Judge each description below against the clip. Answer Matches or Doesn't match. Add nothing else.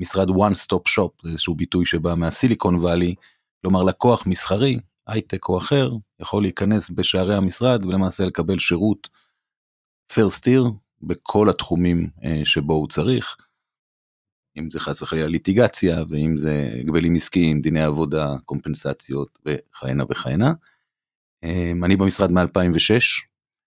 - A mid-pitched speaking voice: Doesn't match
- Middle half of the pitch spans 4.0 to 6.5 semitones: Doesn't match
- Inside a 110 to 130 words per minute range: Matches